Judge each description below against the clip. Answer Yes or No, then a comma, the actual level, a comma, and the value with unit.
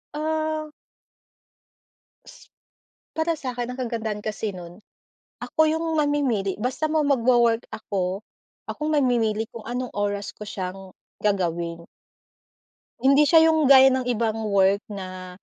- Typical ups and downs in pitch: No, wide, 6.1 semitones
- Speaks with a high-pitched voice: Yes, high, 235 Hz